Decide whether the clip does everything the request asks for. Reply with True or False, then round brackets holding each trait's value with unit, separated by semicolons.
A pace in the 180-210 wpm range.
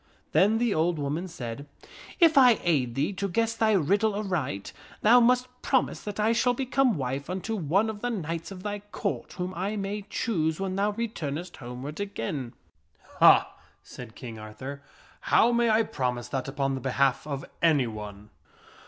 True (185 wpm)